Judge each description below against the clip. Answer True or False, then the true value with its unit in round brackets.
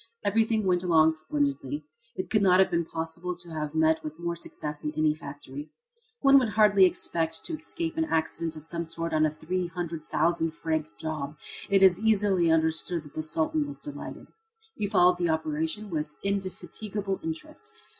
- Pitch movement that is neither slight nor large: True (3.7 semitones)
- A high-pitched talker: False (170 Hz)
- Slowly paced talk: False (175 wpm)